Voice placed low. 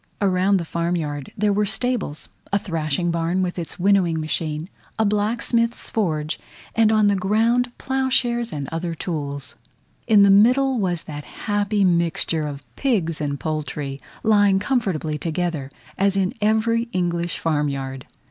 No: medium, 185 Hz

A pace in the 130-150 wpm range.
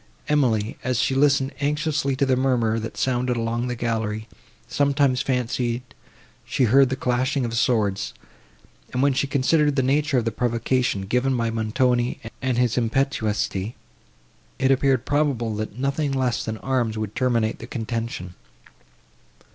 Yes: average, 145 wpm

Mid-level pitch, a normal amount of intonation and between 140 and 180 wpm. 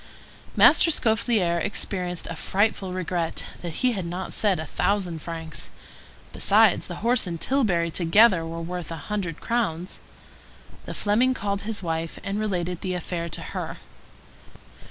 Yes: medium, 180 Hz; average, 3.8 semitones; average, 150 wpm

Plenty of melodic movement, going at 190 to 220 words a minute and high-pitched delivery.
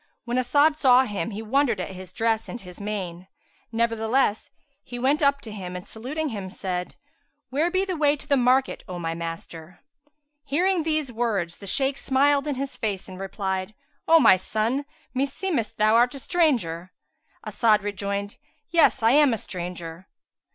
No: wide, 6.6 semitones; average, 170 wpm; high, 230 Hz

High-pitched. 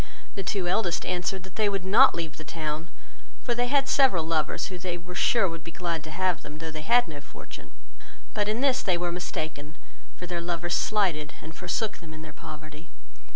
No: medium, 175 Hz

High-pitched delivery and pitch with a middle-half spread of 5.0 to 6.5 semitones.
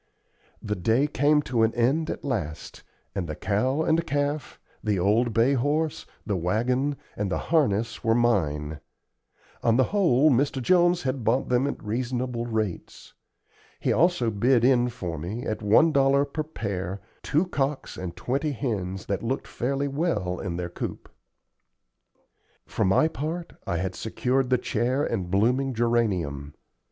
No: low, 120 Hz; wide, 5.6 semitones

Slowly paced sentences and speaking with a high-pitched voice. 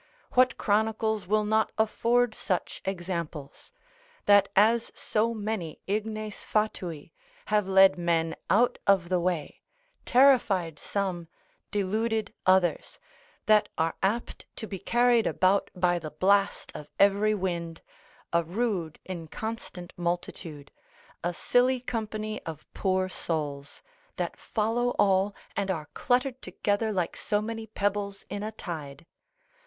Yes: slow, 125 wpm; high, 200 Hz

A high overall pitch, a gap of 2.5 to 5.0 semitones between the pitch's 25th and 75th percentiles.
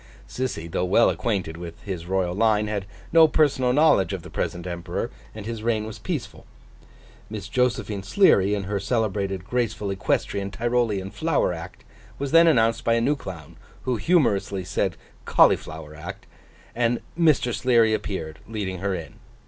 No: low, 105 Hz; average, 4.3 semitones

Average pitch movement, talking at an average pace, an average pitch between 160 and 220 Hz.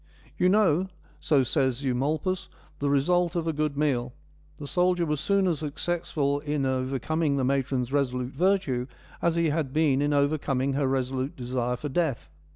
No: average, 3.6 semitones; average, 170 wpm; medium, 145 Hz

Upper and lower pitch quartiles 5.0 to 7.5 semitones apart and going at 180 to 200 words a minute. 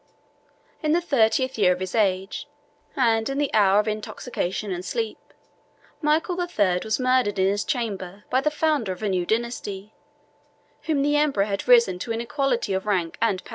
Yes: average, 5.3 semitones; average, 185 wpm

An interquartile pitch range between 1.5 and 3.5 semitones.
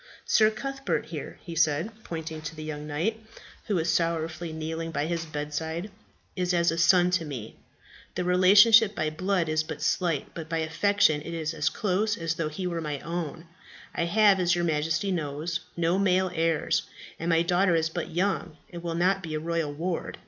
Yes: narrow, 2.5 semitones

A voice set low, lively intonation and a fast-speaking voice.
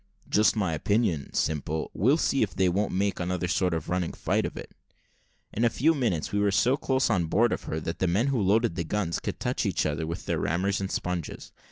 No: very low, 95 Hz; average, 4.6 semitones; fast, 230 wpm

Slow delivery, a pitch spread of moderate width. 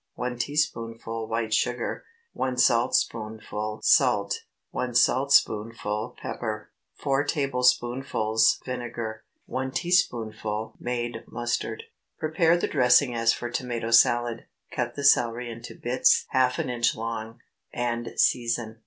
No: slow, 110 wpm; narrow, 1.9 semitones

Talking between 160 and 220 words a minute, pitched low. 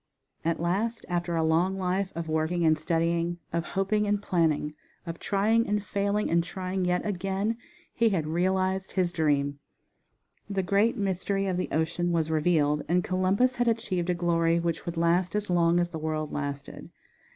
No: average, 175 wpm; medium, 175 Hz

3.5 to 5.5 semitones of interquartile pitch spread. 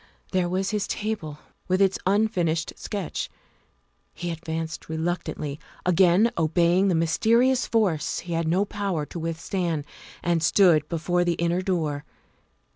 No: average, 3.0 semitones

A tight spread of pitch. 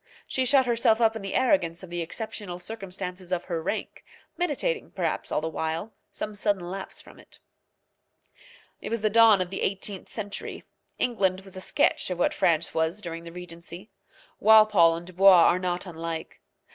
No: average, 3.9 semitones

